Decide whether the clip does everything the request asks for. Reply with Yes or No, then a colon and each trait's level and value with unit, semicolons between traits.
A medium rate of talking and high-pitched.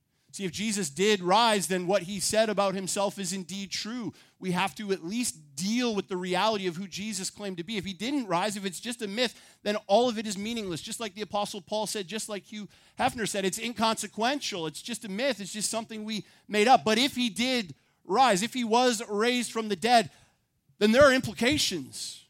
No: fast, 225 wpm; high, 210 Hz